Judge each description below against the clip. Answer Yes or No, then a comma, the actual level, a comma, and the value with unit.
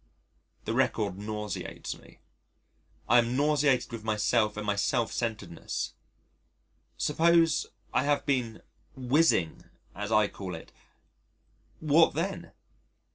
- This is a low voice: Yes, low, 115 Hz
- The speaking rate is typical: No, slow, 110 wpm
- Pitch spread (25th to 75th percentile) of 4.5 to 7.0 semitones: Yes, average, 5.3 semitones